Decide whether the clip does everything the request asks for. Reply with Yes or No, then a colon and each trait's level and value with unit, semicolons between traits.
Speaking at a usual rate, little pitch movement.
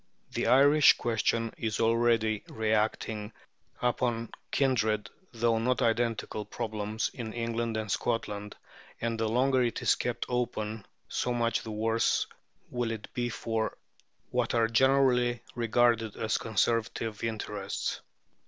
No: slow, 125 wpm; narrow, 1.6 semitones